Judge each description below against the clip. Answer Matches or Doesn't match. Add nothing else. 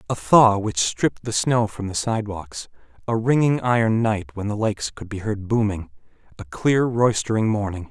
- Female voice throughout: Doesn't match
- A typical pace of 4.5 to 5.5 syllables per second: Matches